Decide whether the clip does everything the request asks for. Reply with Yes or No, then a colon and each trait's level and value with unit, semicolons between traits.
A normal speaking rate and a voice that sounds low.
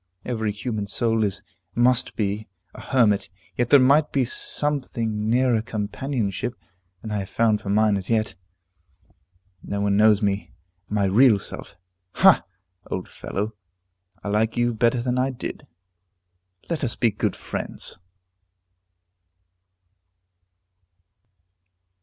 No: slow, 125 wpm; low, 110 Hz